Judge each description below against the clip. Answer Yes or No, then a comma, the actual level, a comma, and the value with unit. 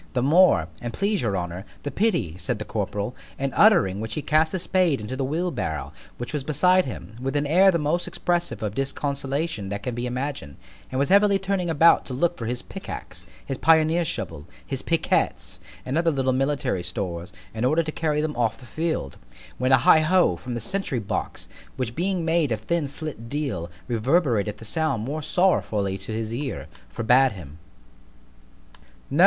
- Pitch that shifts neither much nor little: No, wide, 6.7 semitones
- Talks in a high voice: No, low, 135 Hz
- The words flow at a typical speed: Yes, average, 185 wpm